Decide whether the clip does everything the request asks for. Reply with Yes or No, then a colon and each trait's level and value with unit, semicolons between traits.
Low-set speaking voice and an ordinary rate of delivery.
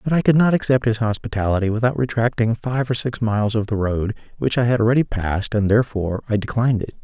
No: low, 115 Hz; fast, 220 wpm